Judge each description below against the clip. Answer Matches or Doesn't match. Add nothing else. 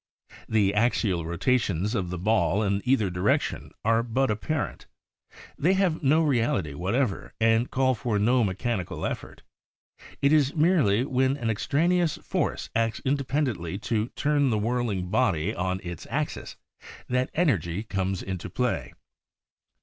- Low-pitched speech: Matches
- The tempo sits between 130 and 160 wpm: Matches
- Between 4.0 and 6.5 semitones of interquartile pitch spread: Matches